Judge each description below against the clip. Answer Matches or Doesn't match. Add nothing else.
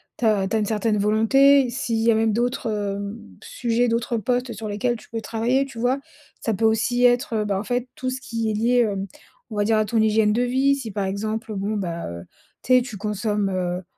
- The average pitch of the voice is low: Doesn't match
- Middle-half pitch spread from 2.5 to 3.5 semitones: Matches